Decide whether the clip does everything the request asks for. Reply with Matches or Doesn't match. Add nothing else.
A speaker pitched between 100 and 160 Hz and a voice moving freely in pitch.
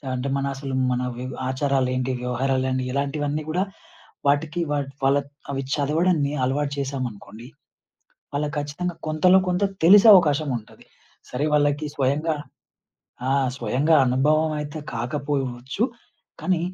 Doesn't match